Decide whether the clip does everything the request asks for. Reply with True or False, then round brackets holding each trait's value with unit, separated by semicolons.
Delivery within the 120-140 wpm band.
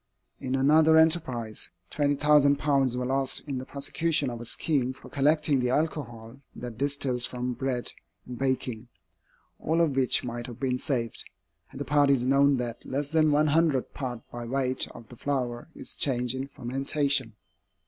False (160 wpm)